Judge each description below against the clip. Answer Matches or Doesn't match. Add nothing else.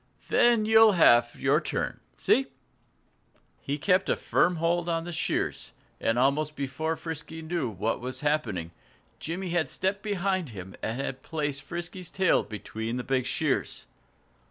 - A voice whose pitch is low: Doesn't match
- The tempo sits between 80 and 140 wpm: Doesn't match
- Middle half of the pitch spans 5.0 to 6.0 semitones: Matches